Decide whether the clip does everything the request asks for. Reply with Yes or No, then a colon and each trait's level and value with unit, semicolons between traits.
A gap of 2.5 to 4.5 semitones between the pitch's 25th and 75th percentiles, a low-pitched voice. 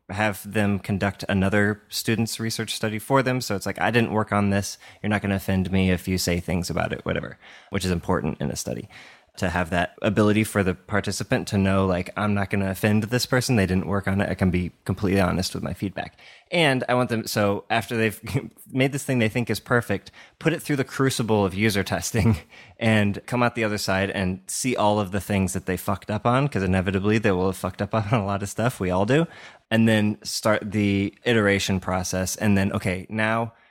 Yes: average, 2.8 semitones; low, 100 Hz